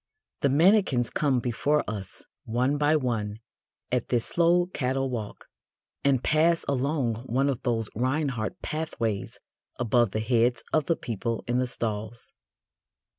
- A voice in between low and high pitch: No, low, 125 Hz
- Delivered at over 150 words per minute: No, slow, 135 wpm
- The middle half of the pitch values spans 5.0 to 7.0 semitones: No, average, 4.2 semitones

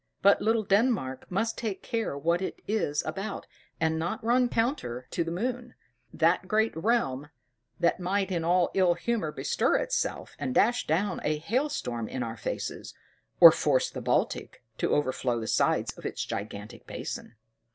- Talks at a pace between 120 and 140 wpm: No, average, 165 wpm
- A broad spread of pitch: Yes, wide, 7.3 semitones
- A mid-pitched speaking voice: Yes, medium, 180 Hz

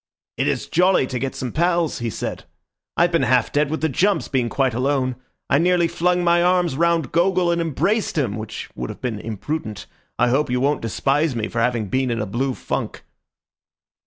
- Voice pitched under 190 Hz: Yes, medium, 140 Hz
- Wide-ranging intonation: Yes, wide, 5.8 semitones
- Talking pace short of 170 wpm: No, average, 200 wpm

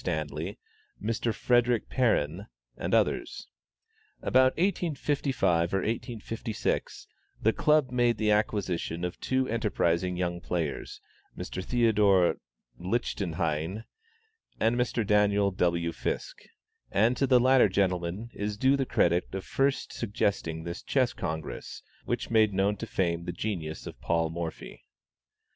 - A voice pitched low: Yes, low, 105 Hz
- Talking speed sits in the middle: No, slow, 125 wpm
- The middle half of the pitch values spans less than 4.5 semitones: No, wide, 5.6 semitones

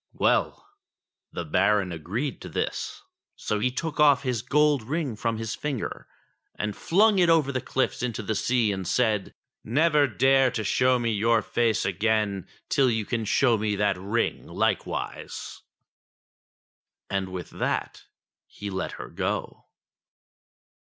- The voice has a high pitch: No, low, 115 Hz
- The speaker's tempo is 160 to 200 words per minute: No, average, 145 wpm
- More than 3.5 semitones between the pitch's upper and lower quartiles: Yes, average, 4.4 semitones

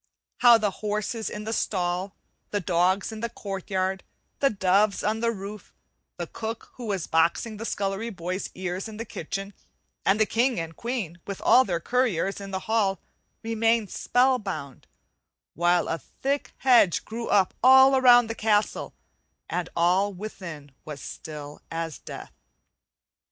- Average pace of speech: Yes, average, 155 wpm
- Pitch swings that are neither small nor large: Yes, average, 4.1 semitones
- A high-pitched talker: Yes, high, 200 Hz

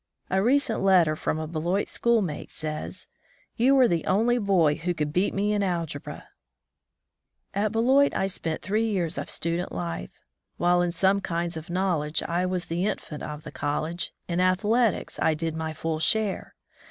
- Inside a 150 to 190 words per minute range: Yes, average, 175 wpm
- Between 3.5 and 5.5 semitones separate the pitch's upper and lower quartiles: Yes, average, 4.1 semitones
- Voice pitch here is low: No, medium, 175 Hz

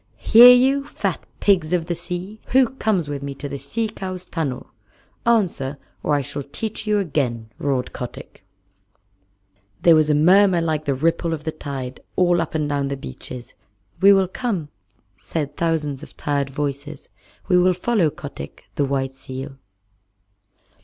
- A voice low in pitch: No, medium, 155 Hz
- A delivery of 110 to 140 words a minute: No, average, 160 wpm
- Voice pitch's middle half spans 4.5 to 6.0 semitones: Yes, average, 4.9 semitones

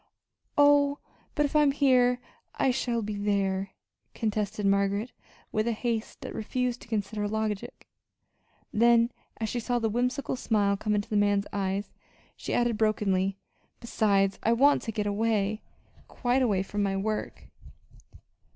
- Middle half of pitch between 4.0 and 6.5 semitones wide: No, average, 3.1 semitones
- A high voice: Yes, high, 215 Hz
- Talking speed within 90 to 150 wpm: Yes, average, 145 wpm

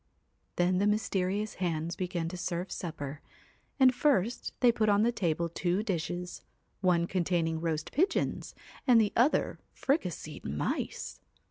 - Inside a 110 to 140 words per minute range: Yes, slow, 135 wpm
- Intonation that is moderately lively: Yes, average, 4.0 semitones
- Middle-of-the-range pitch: Yes, medium, 180 Hz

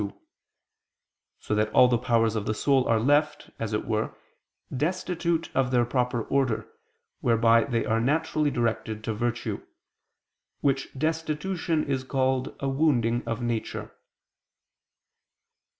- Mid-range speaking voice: No, low, 125 Hz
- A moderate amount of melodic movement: Yes, average, 4.2 semitones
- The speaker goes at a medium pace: No, slow, 130 wpm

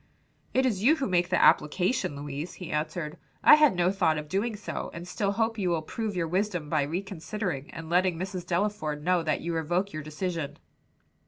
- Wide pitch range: No, average, 4.2 semitones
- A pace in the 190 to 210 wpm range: Yes, average, 195 wpm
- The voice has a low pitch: No, medium, 180 Hz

